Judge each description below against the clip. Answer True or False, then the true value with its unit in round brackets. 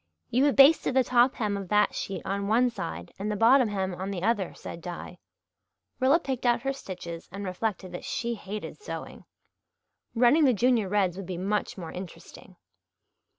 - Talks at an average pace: True (185 wpm)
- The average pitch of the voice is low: False (210 Hz)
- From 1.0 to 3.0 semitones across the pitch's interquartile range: False (4.8 semitones)